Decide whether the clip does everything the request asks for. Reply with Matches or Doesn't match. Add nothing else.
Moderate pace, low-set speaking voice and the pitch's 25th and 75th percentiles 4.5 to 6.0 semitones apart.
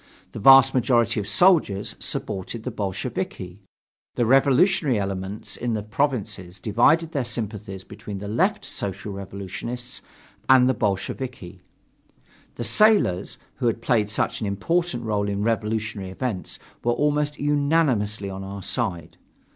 Doesn't match